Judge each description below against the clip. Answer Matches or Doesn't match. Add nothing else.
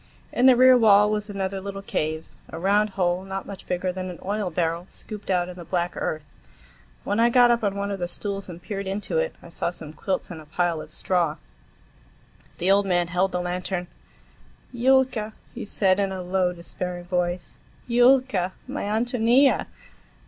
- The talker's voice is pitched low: Doesn't match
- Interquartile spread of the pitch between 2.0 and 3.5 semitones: Matches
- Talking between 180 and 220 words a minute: Matches